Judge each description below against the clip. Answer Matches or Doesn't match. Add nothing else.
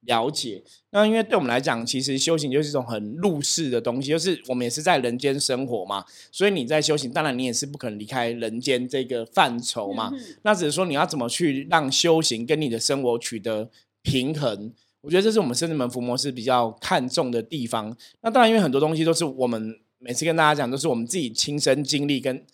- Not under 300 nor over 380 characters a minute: Matches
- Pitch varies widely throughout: Doesn't match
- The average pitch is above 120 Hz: Matches